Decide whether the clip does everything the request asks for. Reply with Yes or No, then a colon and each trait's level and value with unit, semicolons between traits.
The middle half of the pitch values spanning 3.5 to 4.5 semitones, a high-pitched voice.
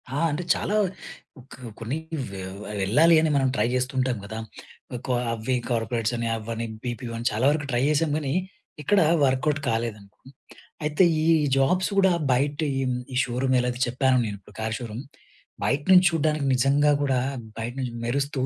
No: average, 3.8 semitones; low, 130 Hz